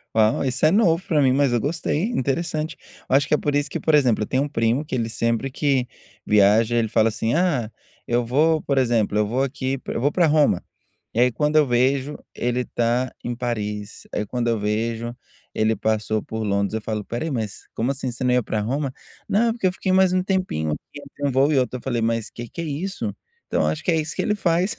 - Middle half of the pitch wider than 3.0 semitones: Yes, average, 4.7 semitones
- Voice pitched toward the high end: No, low, 125 Hz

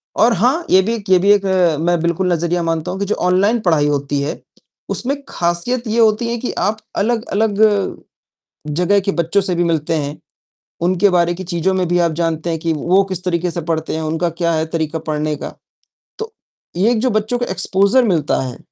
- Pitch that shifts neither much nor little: Yes, average, 3.8 semitones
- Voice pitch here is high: No, medium, 180 Hz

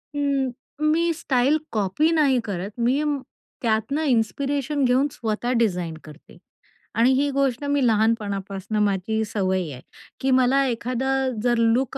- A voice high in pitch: Yes, high, 245 Hz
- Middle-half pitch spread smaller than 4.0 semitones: No, average, 4.5 semitones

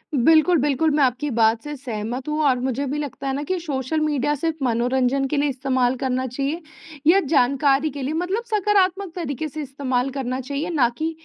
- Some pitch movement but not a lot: Yes, average, 3.3 semitones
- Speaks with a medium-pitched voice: No, very high, 280 Hz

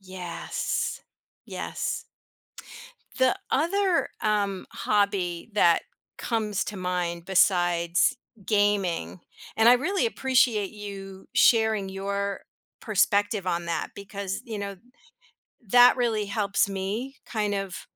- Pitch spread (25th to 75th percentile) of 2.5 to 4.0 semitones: Yes, average, 2.8 semitones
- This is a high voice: Yes, high, 200 Hz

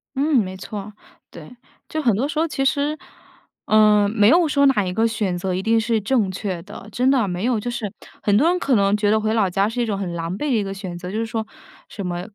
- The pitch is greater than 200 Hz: Yes, high, 215 Hz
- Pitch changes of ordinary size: Yes, average, 4.2 semitones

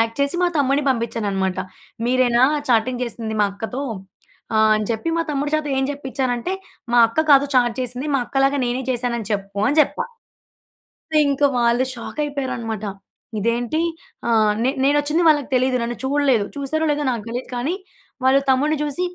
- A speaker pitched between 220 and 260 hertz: Yes, very high, 255 Hz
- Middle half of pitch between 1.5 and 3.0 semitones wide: No, average, 3.6 semitones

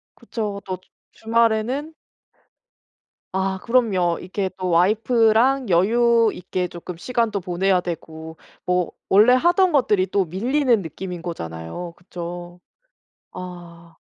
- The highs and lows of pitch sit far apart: No, average, 4.7 semitones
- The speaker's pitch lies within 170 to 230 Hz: Yes, high, 190 Hz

